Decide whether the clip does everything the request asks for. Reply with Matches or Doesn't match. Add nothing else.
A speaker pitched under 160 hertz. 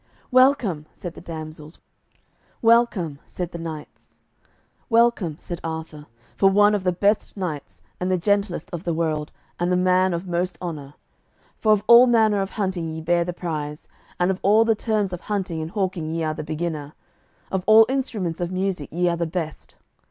Doesn't match